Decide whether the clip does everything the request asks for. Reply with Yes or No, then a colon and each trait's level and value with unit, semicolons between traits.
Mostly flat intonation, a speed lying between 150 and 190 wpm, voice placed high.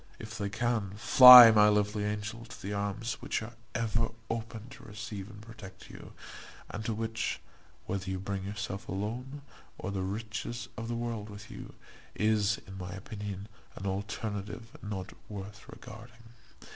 No: narrow, 2.2 semitones; average, 160 wpm; low, 105 Hz